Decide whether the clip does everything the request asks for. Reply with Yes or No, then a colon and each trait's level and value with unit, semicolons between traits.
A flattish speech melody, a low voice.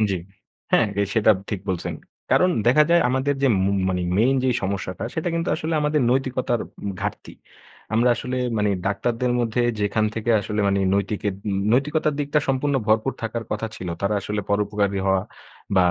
No: average, 4.6 semitones; low, 110 Hz